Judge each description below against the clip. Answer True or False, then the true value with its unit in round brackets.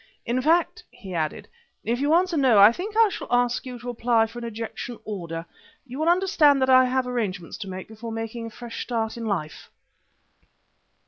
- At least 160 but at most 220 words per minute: True (195 wpm)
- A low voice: False (240 Hz)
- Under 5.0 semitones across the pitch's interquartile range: True (3.0 semitones)